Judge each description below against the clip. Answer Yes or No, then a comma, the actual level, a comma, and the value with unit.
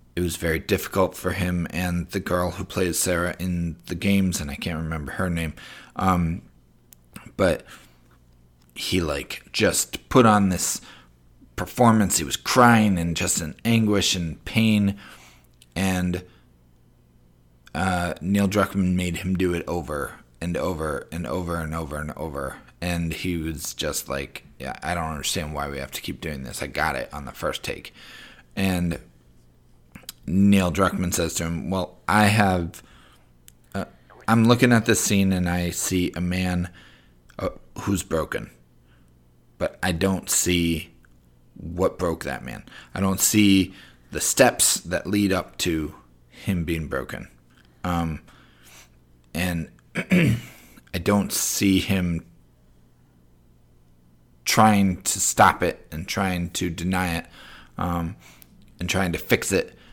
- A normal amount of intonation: No, wide, 7.2 semitones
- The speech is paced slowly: No, average, 145 wpm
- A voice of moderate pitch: No, very low, 85 Hz